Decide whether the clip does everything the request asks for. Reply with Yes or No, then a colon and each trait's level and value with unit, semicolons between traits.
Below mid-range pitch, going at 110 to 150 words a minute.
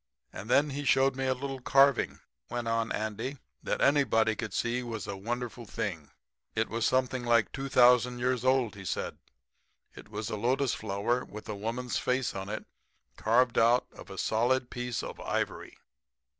No: low, 120 Hz; average, 170 wpm